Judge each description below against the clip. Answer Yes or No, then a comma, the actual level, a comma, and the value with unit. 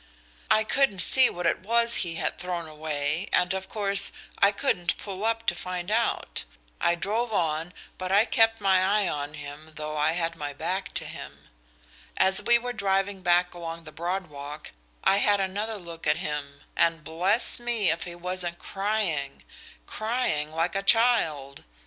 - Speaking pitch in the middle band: Yes, medium, 180 Hz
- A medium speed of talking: Yes, average, 175 wpm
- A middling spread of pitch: Yes, average, 4.3 semitones